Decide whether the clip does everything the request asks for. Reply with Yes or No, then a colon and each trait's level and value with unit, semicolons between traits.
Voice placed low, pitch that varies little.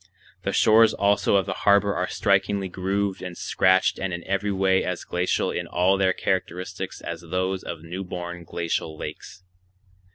Yes: very low, 95 Hz; narrow, 1.7 semitones